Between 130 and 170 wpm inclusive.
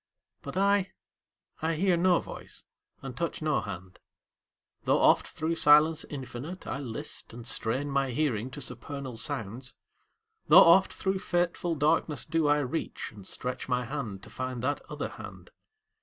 Yes: average, 155 wpm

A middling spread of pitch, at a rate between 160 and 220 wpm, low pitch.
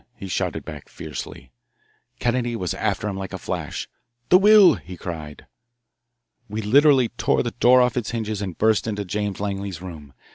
Yes: average, 4.2 semitones; average, 170 wpm; low, 105 Hz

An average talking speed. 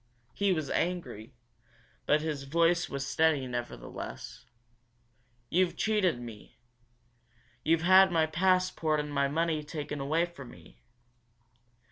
No: slow, 110 wpm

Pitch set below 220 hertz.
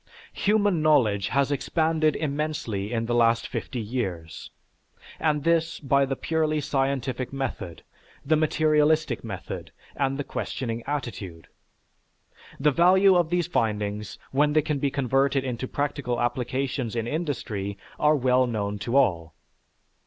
Yes: low, 135 Hz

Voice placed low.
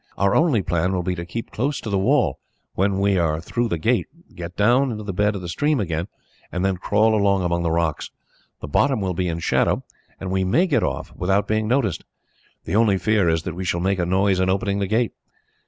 Yes: very low, 95 Hz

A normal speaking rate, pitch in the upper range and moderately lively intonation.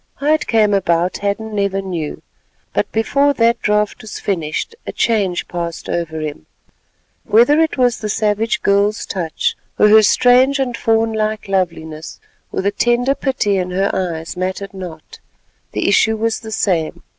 Yes: average, 155 wpm; high, 205 Hz; average, 4.0 semitones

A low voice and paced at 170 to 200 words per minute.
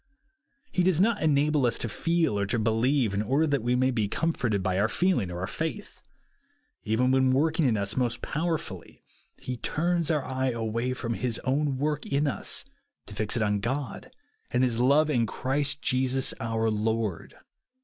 Yes: low, 130 Hz; average, 180 wpm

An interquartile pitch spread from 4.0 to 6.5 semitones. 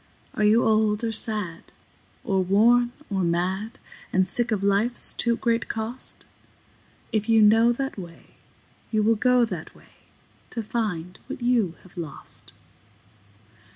No: average, 3.4 semitones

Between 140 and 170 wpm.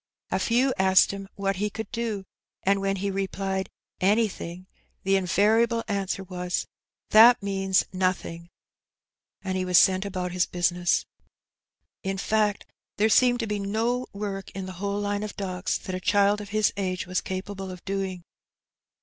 Yes: average, 165 wpm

